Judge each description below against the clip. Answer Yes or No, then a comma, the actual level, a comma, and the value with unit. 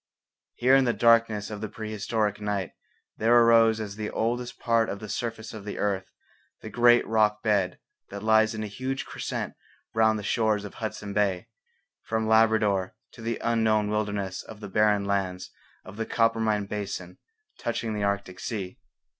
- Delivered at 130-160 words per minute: No, average, 170 wpm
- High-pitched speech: No, low, 110 Hz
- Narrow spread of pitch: Yes, narrow, 1.9 semitones